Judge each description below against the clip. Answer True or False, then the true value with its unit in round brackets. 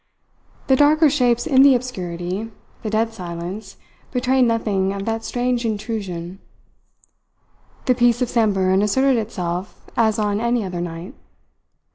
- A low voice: False (220 Hz)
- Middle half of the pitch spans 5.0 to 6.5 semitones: False (4.4 semitones)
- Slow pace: True (130 wpm)